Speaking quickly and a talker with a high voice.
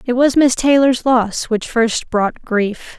No: average, 180 wpm; high, 240 Hz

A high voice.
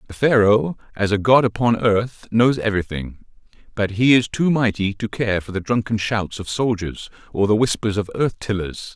No: low, 110 Hz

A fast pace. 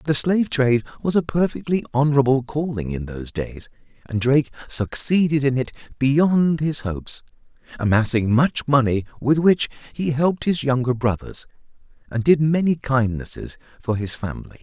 No: average, 150 wpm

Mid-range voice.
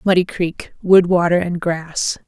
Yes: medium, 175 Hz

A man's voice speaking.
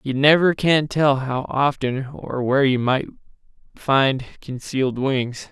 Yes: male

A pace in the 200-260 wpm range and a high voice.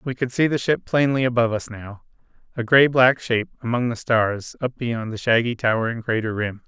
No: fast, 205 wpm; low, 120 Hz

